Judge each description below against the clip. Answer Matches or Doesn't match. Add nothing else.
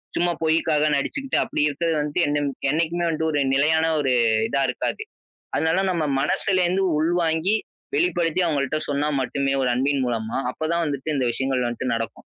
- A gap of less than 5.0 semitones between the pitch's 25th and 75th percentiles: Matches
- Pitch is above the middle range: Doesn't match